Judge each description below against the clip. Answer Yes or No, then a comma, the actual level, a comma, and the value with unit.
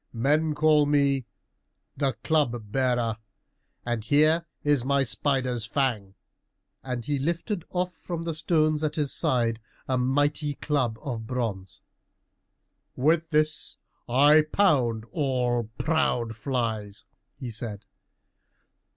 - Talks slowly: Yes, slow, 115 wpm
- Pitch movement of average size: Yes, average, 4.4 semitones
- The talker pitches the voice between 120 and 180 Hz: Yes, low, 135 Hz